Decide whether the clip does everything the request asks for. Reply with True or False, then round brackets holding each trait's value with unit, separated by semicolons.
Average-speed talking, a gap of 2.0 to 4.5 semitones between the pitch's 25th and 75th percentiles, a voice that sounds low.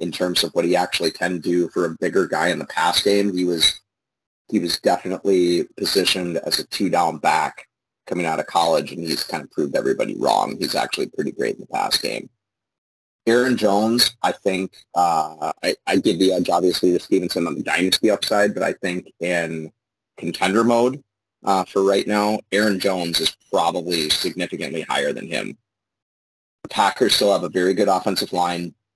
True (180 wpm; 3.7 semitones; 100 Hz)